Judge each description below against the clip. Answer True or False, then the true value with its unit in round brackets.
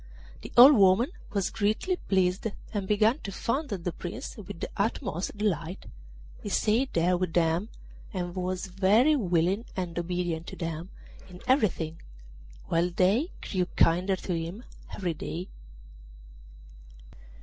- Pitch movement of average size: True (3.5 semitones)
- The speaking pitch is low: False (185 Hz)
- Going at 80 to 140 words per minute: True (135 wpm)